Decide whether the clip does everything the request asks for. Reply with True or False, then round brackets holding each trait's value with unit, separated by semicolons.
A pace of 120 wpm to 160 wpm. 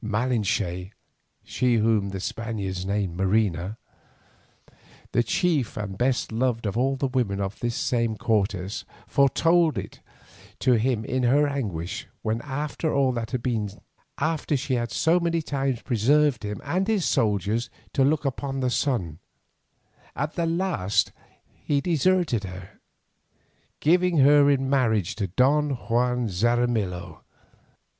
True (135 wpm)